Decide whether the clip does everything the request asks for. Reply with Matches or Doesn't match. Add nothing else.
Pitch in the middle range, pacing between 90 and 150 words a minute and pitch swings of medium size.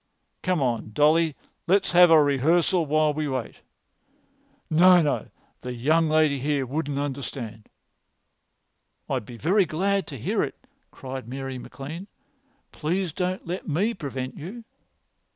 Matches